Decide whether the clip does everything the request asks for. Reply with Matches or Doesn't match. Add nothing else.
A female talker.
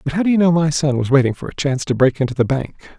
Doesn't match